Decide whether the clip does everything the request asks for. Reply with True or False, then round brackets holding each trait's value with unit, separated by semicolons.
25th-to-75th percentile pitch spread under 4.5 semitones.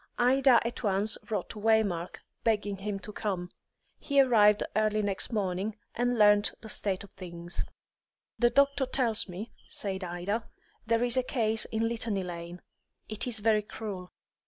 True (3.0 semitones)